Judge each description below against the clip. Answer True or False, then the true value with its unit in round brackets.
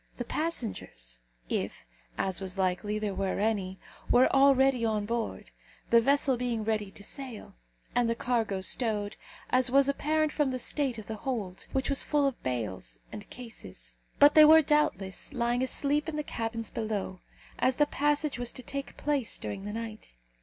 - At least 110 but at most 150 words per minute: False (175 wpm)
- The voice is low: False (235 Hz)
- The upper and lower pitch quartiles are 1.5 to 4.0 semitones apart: False (5.1 semitones)